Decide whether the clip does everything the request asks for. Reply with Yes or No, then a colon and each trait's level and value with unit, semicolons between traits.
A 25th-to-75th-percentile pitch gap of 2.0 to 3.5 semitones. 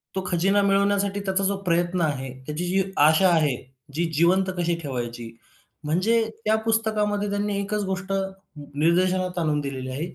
No: average, 4.9 semitones